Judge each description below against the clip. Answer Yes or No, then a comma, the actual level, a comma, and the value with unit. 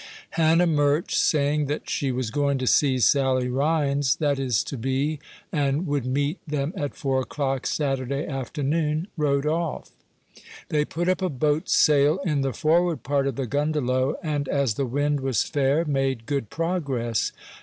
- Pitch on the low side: No, medium, 145 Hz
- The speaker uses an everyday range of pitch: No, narrow, 2.2 semitones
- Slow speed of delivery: No, average, 165 wpm